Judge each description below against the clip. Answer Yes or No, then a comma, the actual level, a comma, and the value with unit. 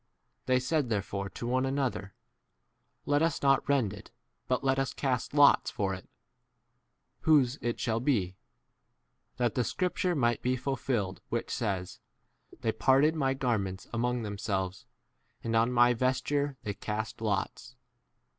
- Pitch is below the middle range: Yes, low, 125 Hz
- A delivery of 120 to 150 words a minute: Yes, average, 140 wpm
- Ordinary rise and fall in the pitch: Yes, average, 4.2 semitones